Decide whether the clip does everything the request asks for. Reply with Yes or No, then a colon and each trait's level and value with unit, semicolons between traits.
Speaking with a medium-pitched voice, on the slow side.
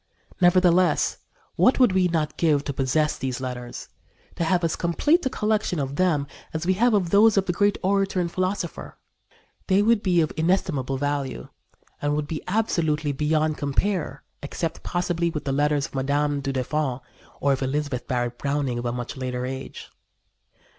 No: medium, 155 Hz; average, 175 wpm